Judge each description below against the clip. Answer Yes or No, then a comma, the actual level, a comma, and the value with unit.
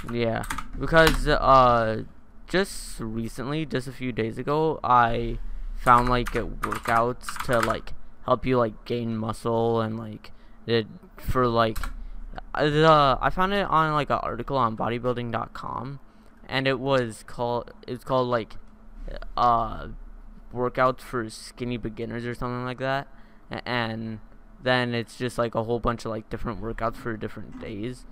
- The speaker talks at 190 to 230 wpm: No, average, 145 wpm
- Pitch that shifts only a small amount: Yes, narrow, 2.1 semitones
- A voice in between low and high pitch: No, low, 120 Hz